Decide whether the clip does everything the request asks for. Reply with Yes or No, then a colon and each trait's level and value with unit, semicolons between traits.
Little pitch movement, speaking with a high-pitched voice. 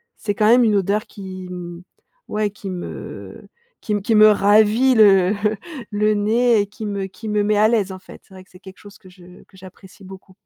Yes: narrow, 2.2 semitones; high, 205 Hz